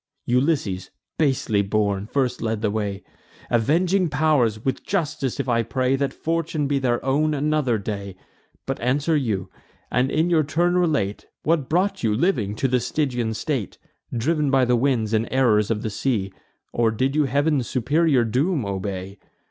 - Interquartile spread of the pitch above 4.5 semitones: Yes, wide, 5.4 semitones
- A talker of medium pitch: No, low, 130 Hz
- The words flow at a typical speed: Yes, average, 165 wpm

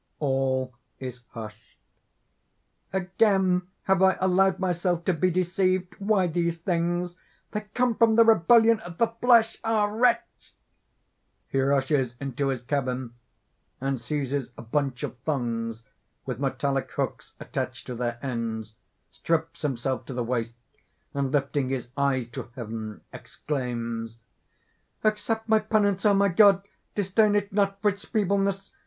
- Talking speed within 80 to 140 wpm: Yes, slow, 135 wpm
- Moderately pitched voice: Yes, medium, 165 Hz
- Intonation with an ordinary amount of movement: No, wide, 7.4 semitones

